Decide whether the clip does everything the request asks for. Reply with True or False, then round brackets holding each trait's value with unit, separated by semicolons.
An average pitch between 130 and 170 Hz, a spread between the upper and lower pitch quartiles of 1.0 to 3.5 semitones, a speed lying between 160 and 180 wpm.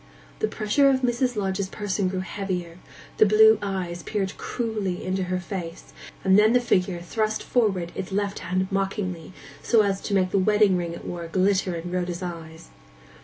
False (190 Hz; 2.8 semitones; 175 wpm)